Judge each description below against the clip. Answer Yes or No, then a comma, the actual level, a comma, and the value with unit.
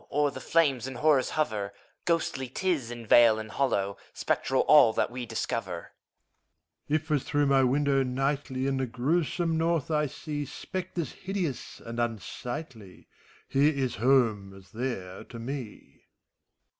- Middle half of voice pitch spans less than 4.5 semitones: Yes, average, 4.1 semitones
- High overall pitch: No, low, 130 Hz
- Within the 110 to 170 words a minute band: Yes, average, 150 wpm